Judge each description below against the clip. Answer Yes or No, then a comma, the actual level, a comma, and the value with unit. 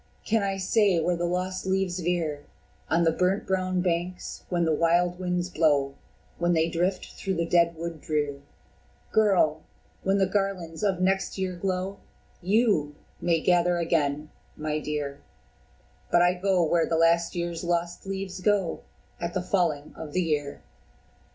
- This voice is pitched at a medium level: Yes, medium, 175 Hz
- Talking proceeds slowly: No, average, 155 wpm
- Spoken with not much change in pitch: Yes, narrow, 2.3 semitones